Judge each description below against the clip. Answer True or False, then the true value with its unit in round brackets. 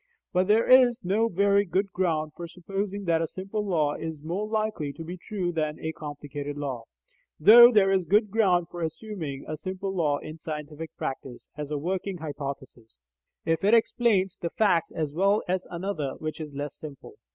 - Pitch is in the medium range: True (175 Hz)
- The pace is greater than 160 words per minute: True (185 wpm)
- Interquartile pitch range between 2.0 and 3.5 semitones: False (4.7 semitones)